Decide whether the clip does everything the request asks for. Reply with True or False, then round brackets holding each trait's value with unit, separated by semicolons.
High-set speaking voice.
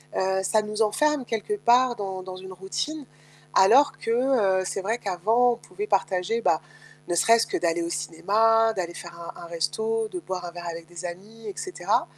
True (200 Hz)